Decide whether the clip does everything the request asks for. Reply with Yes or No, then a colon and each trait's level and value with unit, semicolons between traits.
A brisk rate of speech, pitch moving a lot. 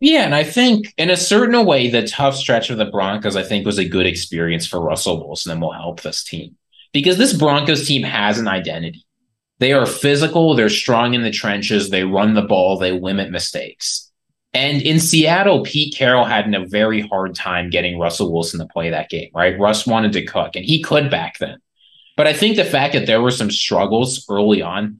Yes: fast, 215 wpm; wide, 7.2 semitones